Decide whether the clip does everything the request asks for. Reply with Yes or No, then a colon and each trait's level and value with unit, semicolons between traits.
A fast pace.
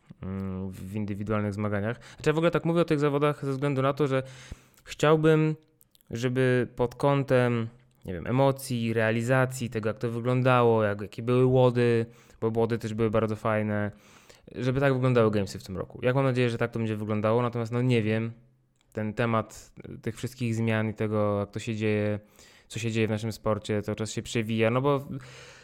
Yes: fast, 190 wpm